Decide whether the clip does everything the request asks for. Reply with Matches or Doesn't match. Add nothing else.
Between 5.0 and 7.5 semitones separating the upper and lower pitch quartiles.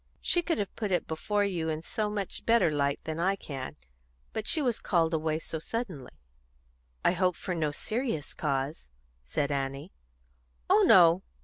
Matches